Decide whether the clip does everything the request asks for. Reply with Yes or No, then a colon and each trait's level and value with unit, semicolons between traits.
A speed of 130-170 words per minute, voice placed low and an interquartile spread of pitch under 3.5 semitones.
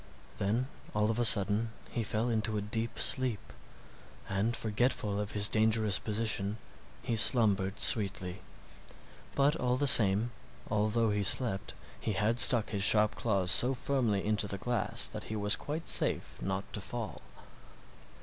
Yes: average, 150 wpm; low, 110 Hz; narrow, 2.4 semitones